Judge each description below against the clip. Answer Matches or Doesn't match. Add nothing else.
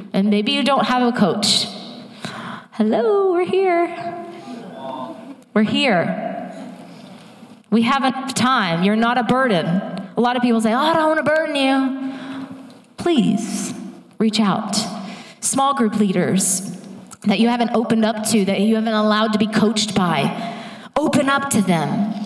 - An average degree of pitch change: Matches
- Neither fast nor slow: Matches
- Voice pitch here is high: Matches